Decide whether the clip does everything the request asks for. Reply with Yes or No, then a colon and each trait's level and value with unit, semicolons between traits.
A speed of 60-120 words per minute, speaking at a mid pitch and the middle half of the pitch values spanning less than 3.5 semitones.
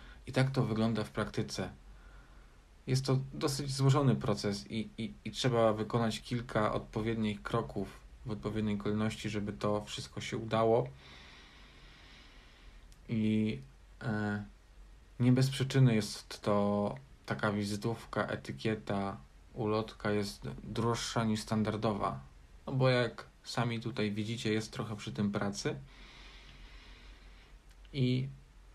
No: average, 115 wpm; low, 110 Hz; narrow, 2.6 semitones